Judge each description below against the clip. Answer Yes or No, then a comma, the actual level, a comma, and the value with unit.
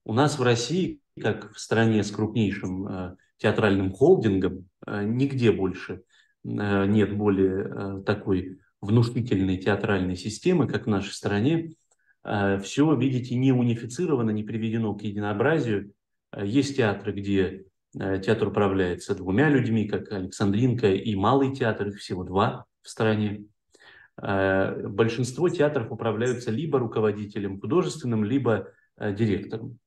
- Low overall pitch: Yes, low, 105 Hz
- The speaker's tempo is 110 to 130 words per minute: Yes, average, 115 wpm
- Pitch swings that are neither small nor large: Yes, average, 3.4 semitones